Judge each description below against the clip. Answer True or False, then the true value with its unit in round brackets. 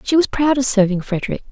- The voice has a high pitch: True (240 Hz)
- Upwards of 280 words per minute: False (240 wpm)